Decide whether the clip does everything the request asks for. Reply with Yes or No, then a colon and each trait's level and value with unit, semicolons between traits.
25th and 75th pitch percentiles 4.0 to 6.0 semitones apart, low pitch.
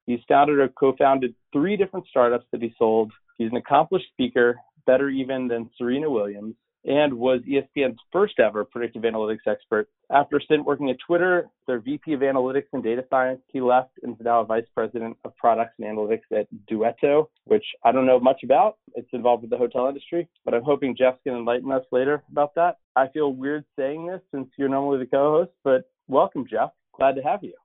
No: average, 3.2 semitones; low, 130 Hz